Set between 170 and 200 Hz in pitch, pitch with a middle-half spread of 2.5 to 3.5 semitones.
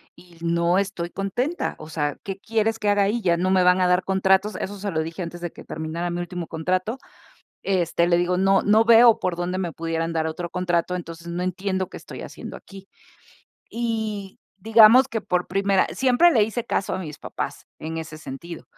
Yes: medium, 185 Hz; average, 3.1 semitones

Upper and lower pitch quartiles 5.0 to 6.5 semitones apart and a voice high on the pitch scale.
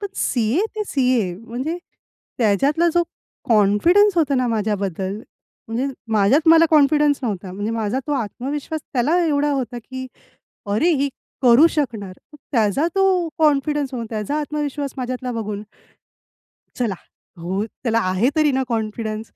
Yes: wide, 5.5 semitones; very high, 255 Hz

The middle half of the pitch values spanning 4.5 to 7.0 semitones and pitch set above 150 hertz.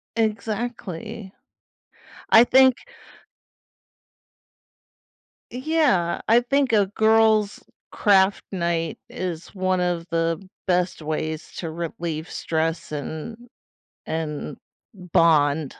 Yes: average, 5.2 semitones; medium, 185 Hz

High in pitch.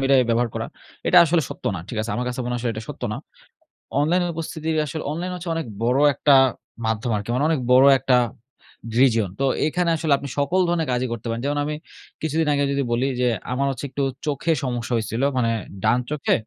No: low, 135 Hz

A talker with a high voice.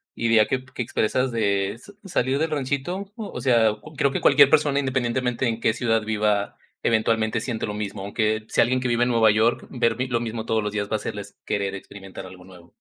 No: low, 115 Hz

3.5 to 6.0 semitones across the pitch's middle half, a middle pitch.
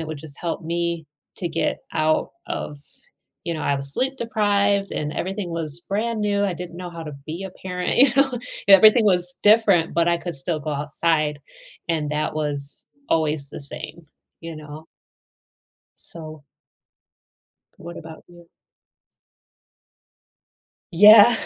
Yes: average, 4.2 semitones; medium, 170 Hz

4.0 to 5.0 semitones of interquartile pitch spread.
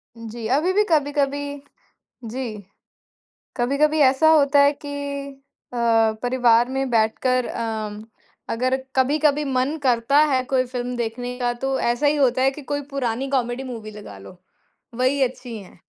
No: average, 2.9 semitones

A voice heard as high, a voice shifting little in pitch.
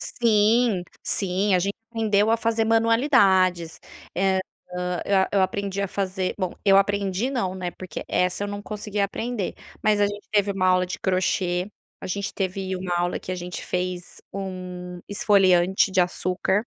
Yes: high, 195 Hz; narrow, 2.0 semitones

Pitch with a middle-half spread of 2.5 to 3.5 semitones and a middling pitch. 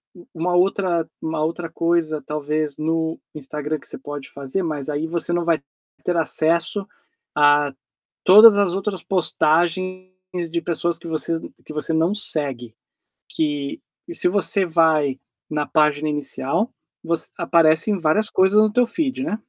Yes: average, 3.1 semitones; medium, 165 Hz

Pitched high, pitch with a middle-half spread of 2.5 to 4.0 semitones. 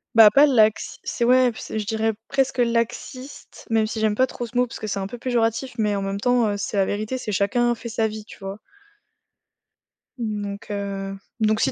Yes: high, 220 Hz; average, 2.8 semitones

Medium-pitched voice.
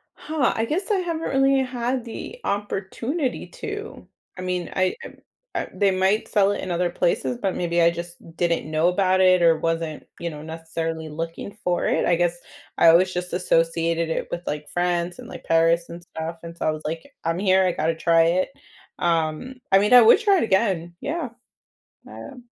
Yes: medium, 175 Hz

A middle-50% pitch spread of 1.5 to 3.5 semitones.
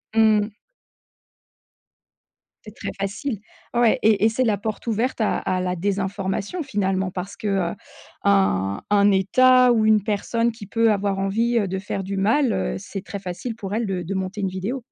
Yes: average, 2.7 semitones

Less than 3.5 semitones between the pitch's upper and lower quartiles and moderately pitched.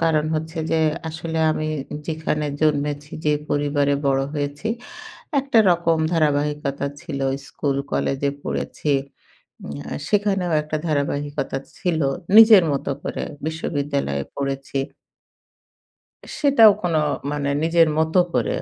Yes: narrow, 2.5 semitones; medium, 150 Hz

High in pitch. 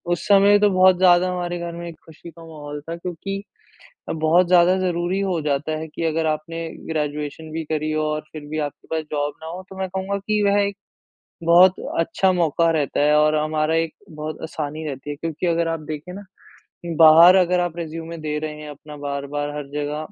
No: medium, 165 Hz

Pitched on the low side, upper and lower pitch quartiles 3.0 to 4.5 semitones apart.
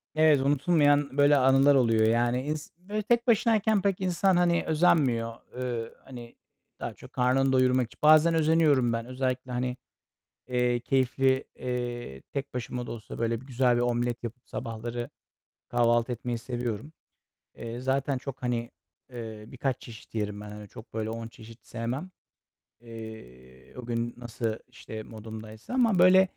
Yes: low, 125 Hz; average, 3.6 semitones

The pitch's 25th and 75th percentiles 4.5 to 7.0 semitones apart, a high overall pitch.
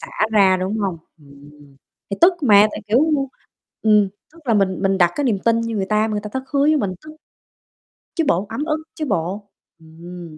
Yes: average, 5.3 semitones; high, 205 Hz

